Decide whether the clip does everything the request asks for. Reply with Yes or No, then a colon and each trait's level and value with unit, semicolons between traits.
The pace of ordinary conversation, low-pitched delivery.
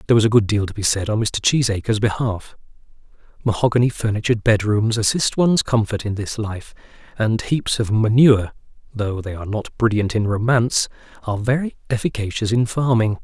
Yes: average, 170 wpm; low, 110 Hz